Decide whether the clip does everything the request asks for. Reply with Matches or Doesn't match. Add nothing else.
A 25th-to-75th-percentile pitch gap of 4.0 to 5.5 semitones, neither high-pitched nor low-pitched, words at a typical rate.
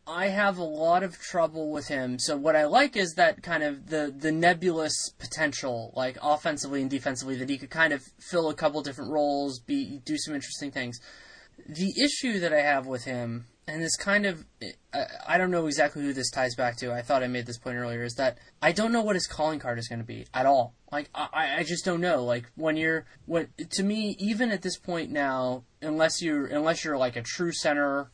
Doesn't match